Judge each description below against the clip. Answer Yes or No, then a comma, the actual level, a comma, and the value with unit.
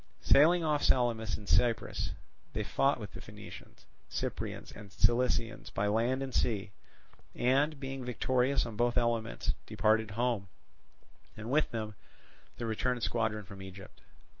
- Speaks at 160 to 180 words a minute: No, average, 140 wpm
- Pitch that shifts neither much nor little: Yes, average, 3.0 semitones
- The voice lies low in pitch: Yes, low, 115 Hz